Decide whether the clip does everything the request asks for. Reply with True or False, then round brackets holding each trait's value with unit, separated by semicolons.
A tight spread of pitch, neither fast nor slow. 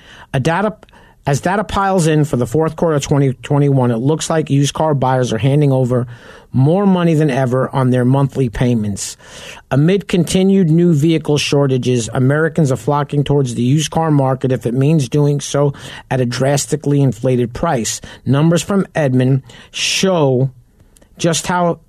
False (3.7 semitones; 160 wpm)